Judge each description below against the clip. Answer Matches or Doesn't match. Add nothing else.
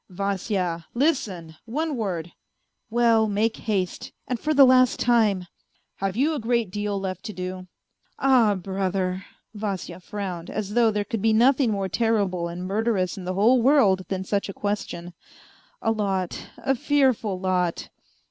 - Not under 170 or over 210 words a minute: Matches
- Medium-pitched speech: Doesn't match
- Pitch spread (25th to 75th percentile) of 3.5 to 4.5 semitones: Matches